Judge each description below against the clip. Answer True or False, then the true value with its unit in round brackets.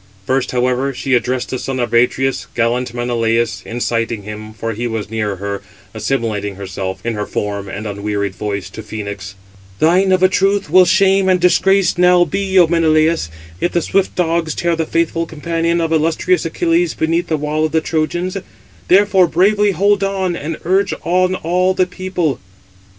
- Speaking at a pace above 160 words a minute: True (170 wpm)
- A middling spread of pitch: False (8.1 semitones)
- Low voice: False (160 Hz)